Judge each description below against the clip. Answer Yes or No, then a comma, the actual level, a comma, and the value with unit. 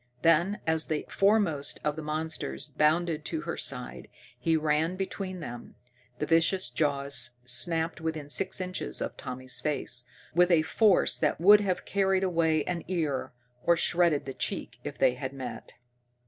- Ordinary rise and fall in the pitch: Yes, average, 3.6 semitones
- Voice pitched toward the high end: No, medium, 160 Hz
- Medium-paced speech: Yes, average, 160 wpm